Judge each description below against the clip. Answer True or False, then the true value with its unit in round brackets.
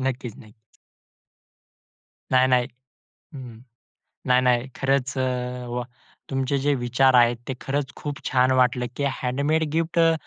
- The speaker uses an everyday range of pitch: False (1.8 semitones)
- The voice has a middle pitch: False (130 Hz)